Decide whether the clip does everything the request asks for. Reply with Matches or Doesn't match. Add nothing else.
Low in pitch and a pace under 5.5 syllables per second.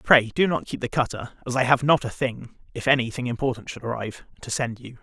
Doesn't match